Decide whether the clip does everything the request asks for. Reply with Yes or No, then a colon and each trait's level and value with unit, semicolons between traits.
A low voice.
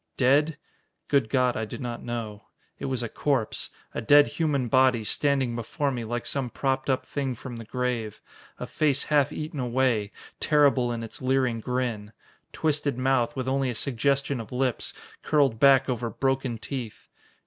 Yes: low, 130 Hz